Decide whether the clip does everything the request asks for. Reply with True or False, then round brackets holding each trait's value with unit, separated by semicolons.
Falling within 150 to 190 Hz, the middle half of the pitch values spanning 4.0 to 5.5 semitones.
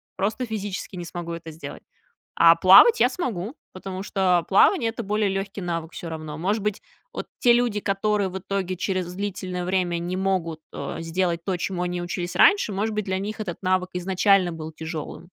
False (185 Hz; 2.6 semitones)